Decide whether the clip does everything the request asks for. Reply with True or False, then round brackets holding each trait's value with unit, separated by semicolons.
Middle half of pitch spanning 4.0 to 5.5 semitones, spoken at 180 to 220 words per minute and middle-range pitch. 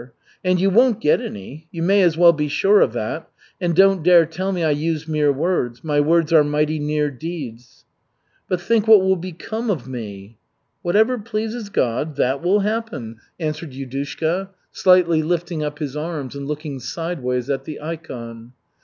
False (4.5 semitones; 170 wpm; 160 Hz)